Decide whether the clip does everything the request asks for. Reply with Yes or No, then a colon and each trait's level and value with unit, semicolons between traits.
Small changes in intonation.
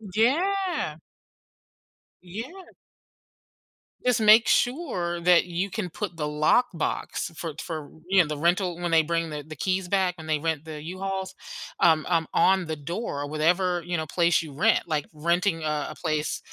No: average, 3.5 semitones